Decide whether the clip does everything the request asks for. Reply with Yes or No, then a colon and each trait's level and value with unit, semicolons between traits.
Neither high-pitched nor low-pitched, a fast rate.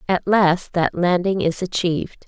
No: medium, 180 Hz; average, 160 wpm